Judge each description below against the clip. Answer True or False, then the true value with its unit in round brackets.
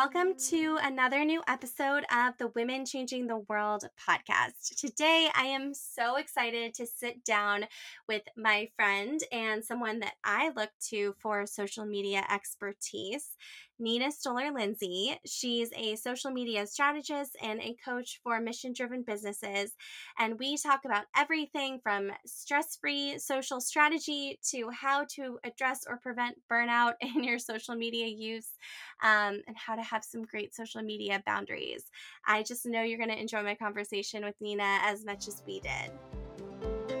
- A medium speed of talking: True (155 wpm)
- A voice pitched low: False (235 Hz)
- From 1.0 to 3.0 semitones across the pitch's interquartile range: False (4.2 semitones)